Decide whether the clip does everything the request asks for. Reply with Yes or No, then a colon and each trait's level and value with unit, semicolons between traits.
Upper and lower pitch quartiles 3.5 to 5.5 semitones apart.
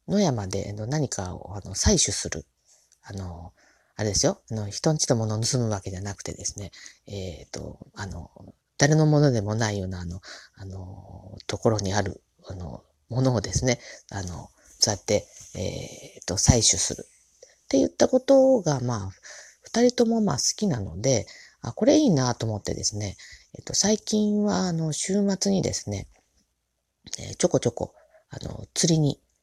No: wide, 8.2 semitones